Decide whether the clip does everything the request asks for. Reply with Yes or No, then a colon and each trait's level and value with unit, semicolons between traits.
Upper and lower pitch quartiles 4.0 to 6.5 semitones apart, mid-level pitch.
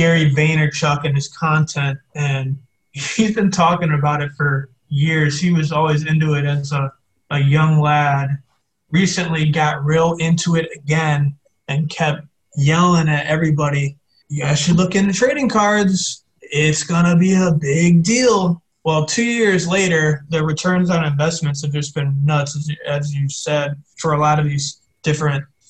No: narrow, 2.6 semitones; medium, 150 Hz